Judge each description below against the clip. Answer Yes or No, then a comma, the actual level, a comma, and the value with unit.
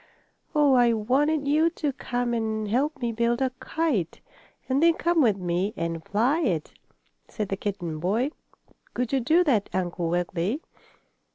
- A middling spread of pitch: No, wide, 6.7 semitones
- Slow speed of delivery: No, average, 160 wpm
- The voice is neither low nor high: No, high, 235 Hz